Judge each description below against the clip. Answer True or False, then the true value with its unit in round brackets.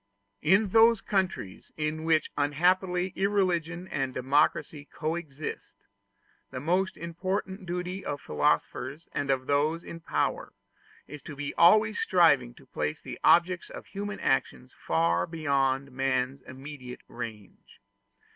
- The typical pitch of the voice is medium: True (155 Hz)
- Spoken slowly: True (125 wpm)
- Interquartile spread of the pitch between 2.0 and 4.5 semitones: False (5.1 semitones)